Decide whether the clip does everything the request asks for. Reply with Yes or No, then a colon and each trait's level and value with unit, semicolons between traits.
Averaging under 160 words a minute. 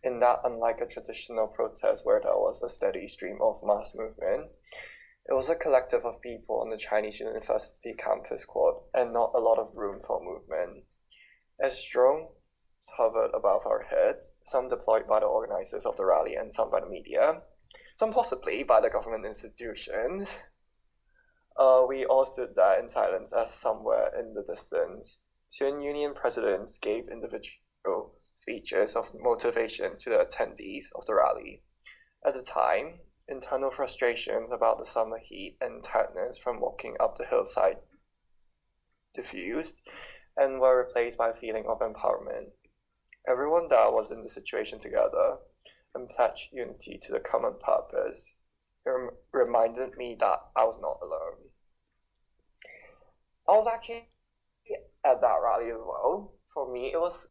Yes: average, 150 wpm